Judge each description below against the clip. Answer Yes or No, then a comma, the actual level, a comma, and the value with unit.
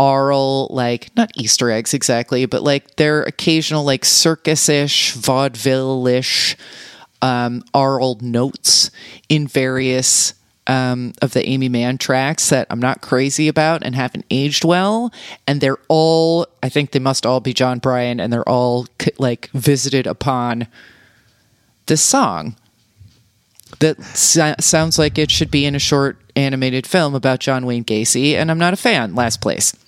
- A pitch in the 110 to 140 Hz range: Yes, low, 135 Hz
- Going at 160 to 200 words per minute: No, average, 150 wpm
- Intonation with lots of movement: No, average, 3.2 semitones